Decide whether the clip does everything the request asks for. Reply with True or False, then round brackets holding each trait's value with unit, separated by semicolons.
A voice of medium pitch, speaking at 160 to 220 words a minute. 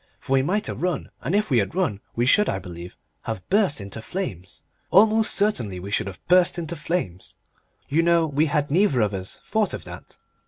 True (145 Hz; 205 wpm)